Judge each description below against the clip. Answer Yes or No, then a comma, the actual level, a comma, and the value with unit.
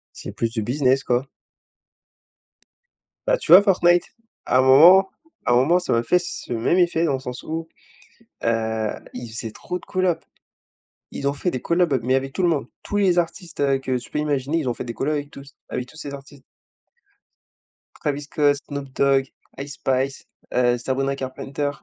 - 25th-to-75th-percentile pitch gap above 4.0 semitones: Yes, average, 4.4 semitones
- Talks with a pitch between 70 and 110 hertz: No, medium, 140 Hz